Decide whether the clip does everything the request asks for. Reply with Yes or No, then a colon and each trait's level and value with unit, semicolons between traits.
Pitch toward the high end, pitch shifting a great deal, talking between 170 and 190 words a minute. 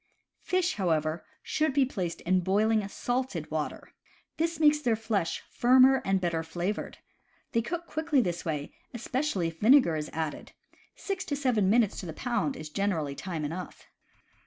No: high, 205 Hz; wide, 7.8 semitones; average, 160 wpm